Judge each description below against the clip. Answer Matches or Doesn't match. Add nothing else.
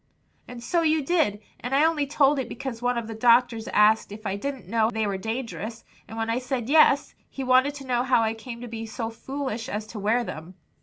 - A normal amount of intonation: Matches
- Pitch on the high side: Matches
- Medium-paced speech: Doesn't match